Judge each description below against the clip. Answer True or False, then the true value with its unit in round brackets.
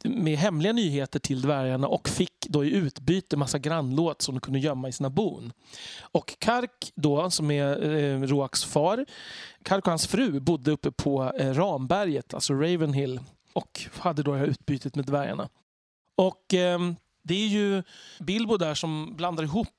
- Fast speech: False (170 wpm)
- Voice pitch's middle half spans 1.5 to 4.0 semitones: False (4.4 semitones)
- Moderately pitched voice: True (155 Hz)